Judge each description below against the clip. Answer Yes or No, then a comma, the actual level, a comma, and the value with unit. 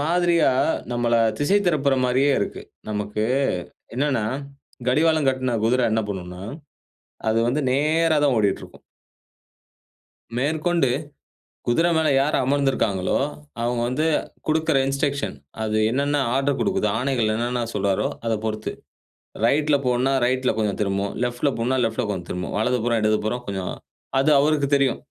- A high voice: No, low, 130 Hz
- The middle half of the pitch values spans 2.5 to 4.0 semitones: No, average, 4.7 semitones